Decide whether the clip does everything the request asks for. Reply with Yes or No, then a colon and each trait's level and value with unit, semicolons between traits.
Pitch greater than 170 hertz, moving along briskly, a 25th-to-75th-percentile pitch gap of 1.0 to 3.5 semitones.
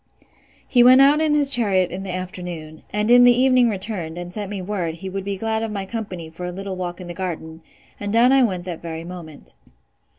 No: high, 190 Hz; fast, 230 wpm; average, 4.4 semitones